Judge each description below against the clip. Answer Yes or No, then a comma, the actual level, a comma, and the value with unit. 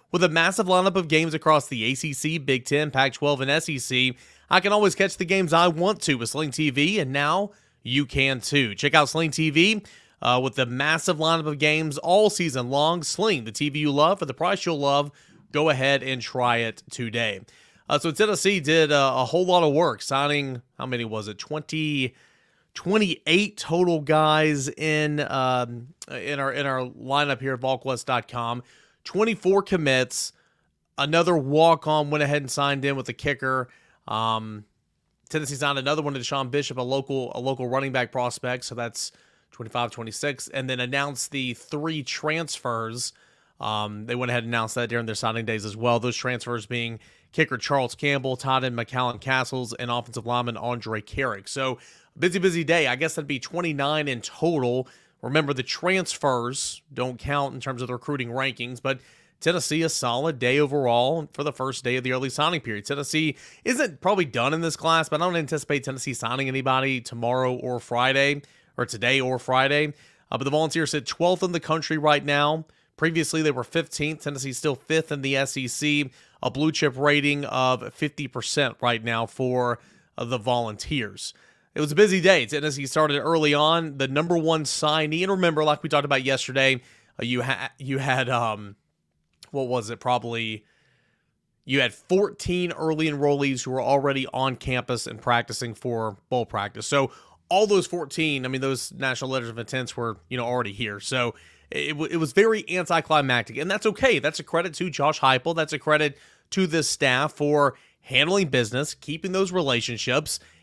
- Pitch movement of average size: Yes, average, 4.0 semitones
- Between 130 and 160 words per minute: No, average, 180 wpm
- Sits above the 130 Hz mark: Yes, medium, 140 Hz